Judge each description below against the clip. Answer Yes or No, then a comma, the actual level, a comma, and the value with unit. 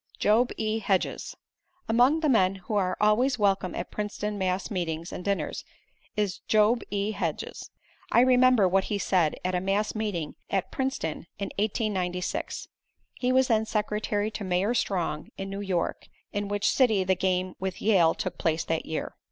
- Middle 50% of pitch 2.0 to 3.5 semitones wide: Yes, average, 3.0 semitones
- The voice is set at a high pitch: Yes, high, 200 Hz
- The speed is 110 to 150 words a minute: No, average, 170 wpm